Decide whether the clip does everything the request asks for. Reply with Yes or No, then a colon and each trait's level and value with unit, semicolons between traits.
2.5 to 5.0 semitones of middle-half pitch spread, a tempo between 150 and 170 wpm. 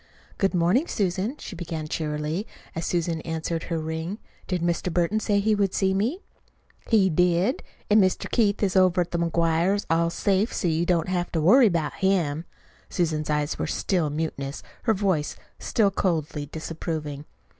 Yes: average, 3.3 semitones; average, 165 wpm